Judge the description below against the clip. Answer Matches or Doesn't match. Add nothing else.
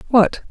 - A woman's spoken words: Matches